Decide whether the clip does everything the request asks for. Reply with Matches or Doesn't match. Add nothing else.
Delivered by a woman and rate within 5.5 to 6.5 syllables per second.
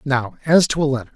Doesn't match